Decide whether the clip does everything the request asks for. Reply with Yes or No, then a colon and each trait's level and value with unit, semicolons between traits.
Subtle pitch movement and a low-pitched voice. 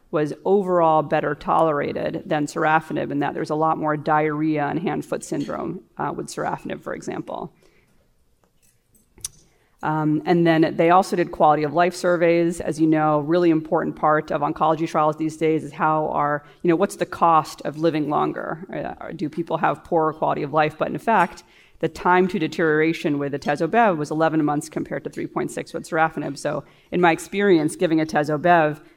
No: narrow, 1.8 semitones; medium, 160 Hz